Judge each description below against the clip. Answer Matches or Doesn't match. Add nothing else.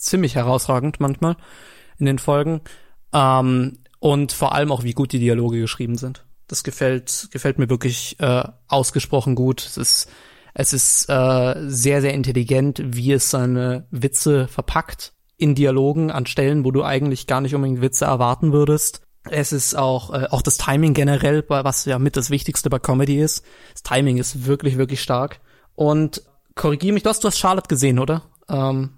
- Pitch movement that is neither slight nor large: Doesn't match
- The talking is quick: Doesn't match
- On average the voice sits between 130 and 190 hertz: Matches